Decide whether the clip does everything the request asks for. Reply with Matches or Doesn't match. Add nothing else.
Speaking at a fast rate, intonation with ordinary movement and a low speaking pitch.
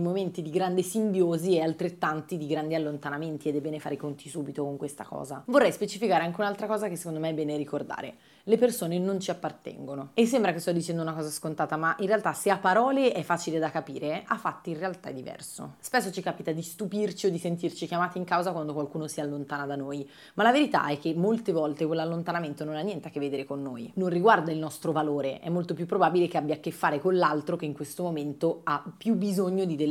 Doesn't match